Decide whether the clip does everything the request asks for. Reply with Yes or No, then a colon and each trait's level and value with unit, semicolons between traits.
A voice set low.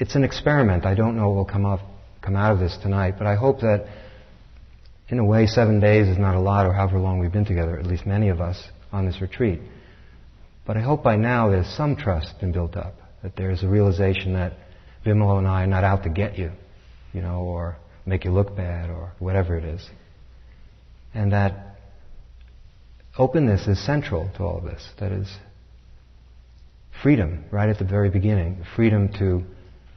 Yes: very low, 95 Hz